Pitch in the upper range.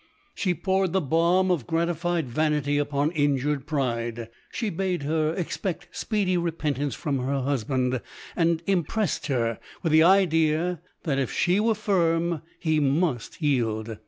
No: medium, 155 Hz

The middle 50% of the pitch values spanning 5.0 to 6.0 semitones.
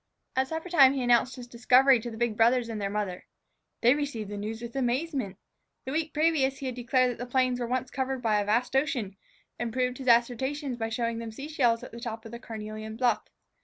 No: average, 2.7 semitones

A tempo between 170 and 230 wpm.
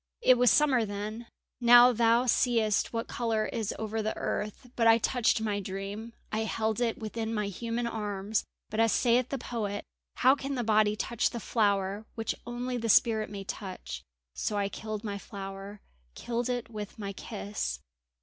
Yes: average, 175 wpm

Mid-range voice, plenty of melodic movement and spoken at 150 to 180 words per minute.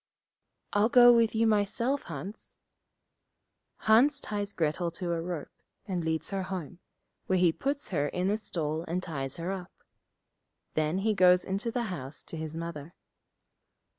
No: medium, 180 Hz; average, 4.7 semitones; average, 155 wpm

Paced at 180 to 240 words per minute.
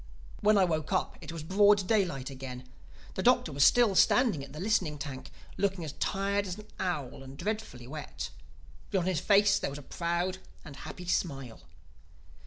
Yes: average, 185 wpm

